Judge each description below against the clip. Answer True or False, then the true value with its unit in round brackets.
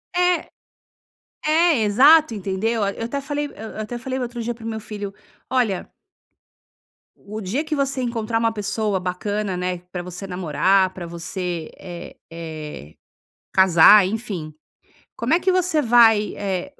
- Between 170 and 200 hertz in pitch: False (215 Hz)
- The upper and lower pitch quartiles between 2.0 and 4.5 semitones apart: False (5.1 semitones)